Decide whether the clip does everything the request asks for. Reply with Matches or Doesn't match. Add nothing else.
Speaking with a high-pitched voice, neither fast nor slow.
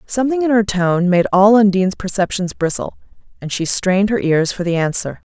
Matches